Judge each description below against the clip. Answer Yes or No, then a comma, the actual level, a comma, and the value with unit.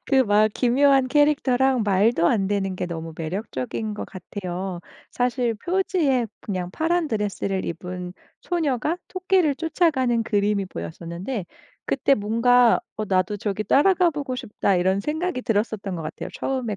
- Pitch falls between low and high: No, high, 220 Hz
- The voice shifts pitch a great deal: Yes, wide, 6.1 semitones